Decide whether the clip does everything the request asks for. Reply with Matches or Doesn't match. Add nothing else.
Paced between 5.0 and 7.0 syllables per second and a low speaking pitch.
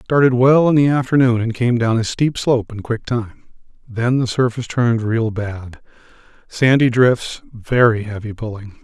Doesn't match